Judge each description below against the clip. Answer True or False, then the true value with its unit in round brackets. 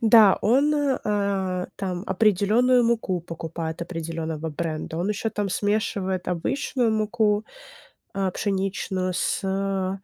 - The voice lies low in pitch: False (195 Hz)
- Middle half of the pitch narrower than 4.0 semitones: True (3.2 semitones)